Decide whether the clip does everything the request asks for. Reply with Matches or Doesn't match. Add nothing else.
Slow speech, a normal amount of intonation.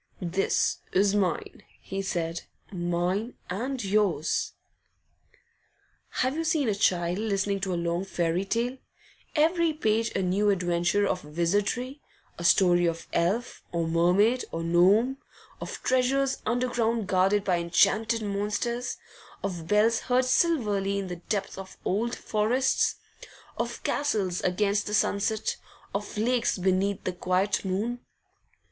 Matches